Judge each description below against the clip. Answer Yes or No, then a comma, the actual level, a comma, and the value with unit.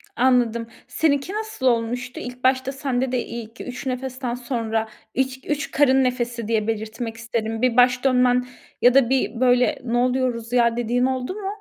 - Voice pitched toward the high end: Yes, very high, 250 Hz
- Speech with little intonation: Yes, narrow, 1.9 semitones